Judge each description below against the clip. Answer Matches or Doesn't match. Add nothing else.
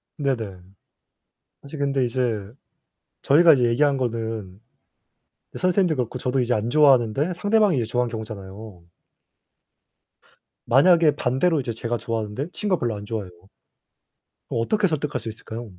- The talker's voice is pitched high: Doesn't match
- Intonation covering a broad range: Doesn't match